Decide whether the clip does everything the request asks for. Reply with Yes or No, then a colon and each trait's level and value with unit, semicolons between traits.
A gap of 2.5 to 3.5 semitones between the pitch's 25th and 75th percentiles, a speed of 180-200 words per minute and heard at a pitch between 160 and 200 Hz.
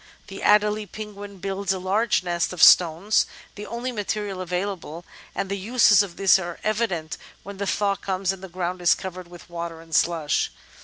Yes: average, 2.8 semitones; average, 185 wpm; high, 190 Hz